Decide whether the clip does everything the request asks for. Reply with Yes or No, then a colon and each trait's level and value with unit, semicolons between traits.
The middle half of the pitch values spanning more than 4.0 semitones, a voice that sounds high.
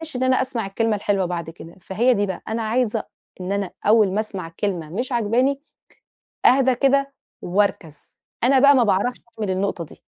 Yes: average, 4.8 semitones; high, 215 Hz